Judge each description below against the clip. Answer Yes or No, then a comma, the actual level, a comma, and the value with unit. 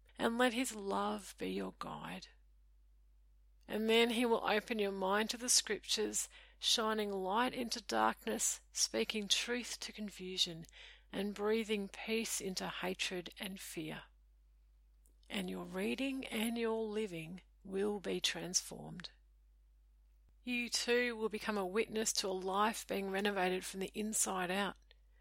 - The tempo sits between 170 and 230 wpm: No, slow, 135 wpm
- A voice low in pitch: No, high, 200 Hz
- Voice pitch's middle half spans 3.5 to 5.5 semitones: Yes, average, 4.2 semitones